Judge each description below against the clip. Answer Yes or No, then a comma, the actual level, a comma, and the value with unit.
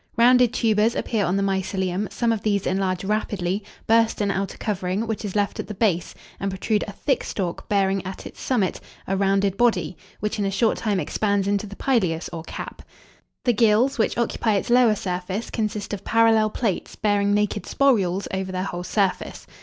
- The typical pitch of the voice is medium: No, high, 205 Hz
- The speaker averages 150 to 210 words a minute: Yes, average, 190 wpm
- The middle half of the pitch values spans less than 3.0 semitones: Yes, narrow, 2.6 semitones